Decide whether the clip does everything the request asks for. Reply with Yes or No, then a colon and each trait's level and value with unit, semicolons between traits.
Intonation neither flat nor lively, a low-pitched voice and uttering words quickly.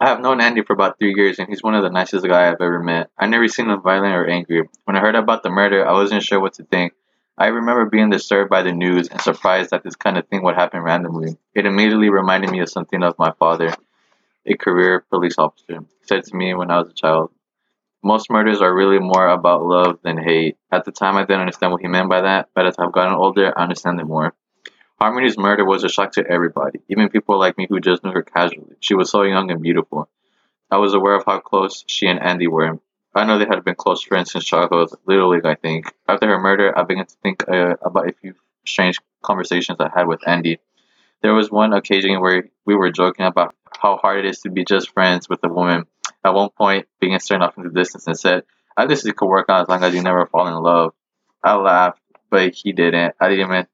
No: narrow, 2.0 semitones; very low, 90 Hz; fast, 245 wpm